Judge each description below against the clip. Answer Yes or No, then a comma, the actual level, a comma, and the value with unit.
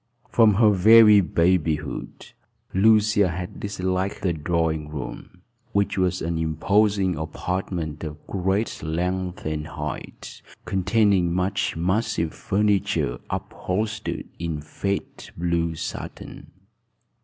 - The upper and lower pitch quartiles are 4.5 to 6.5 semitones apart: No, average, 3.5 semitones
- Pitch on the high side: No, very low, 90 Hz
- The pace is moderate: No, slow, 100 wpm